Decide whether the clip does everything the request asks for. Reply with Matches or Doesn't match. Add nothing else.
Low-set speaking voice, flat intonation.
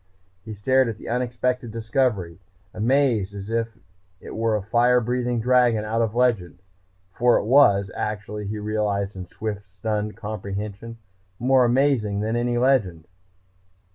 Doesn't match